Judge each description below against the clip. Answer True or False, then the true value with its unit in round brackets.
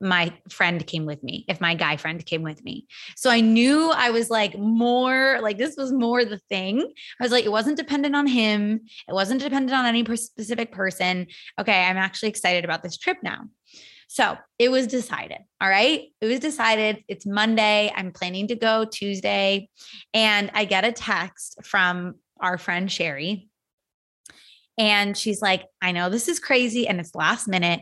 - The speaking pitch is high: True (210 Hz)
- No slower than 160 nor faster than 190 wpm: True (185 wpm)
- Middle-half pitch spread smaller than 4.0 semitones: False (4.5 semitones)